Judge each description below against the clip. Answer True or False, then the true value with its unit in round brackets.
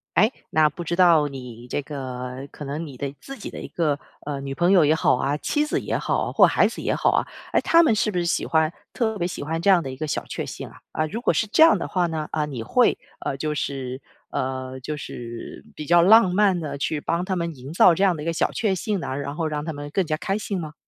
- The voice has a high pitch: False (155 Hz)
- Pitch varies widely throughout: False (4.6 semitones)